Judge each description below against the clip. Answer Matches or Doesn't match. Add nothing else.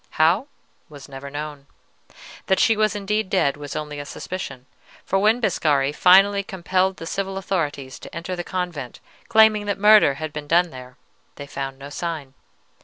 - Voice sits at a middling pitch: Matches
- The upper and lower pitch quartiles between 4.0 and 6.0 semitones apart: Matches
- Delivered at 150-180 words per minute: Matches